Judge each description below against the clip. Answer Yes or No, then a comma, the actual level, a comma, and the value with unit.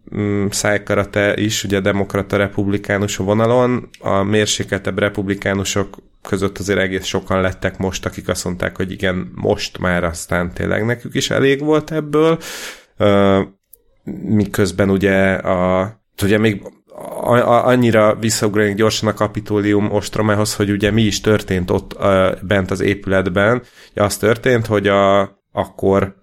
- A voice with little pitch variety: Yes, narrow, 1.6 semitones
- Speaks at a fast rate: No, average, 125 wpm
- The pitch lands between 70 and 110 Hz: Yes, low, 100 Hz